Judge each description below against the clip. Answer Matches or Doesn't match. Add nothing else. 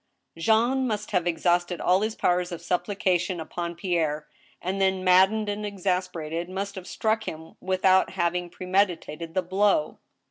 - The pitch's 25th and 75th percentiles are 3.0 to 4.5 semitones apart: Doesn't match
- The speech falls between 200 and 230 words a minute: Doesn't match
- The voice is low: Doesn't match